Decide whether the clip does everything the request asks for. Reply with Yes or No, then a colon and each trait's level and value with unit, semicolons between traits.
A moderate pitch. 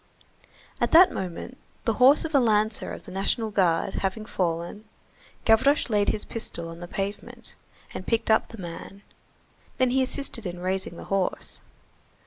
No: high, 210 Hz